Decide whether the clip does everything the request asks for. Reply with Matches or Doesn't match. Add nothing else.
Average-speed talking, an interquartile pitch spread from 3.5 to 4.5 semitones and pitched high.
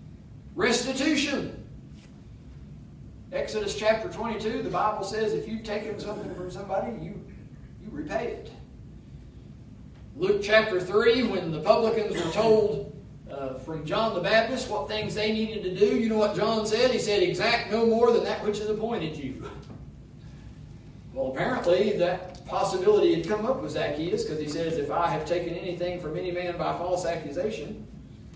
Matches